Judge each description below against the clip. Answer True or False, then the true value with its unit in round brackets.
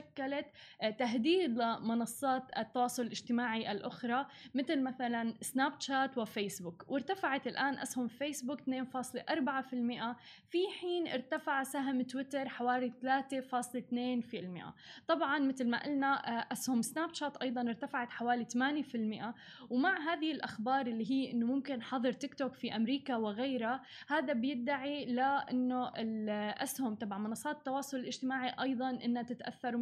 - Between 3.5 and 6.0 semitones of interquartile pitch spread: False (2.4 semitones)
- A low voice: False (255 Hz)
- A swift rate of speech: False (115 wpm)